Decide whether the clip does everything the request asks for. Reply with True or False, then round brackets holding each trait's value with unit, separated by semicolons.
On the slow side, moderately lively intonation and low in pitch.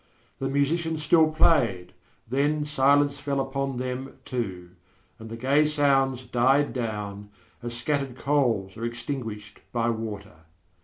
True (125 wpm; 3.9 semitones; 130 Hz)